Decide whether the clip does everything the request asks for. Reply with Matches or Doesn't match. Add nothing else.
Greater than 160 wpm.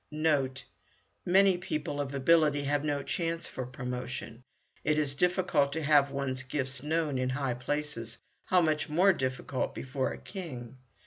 Doesn't match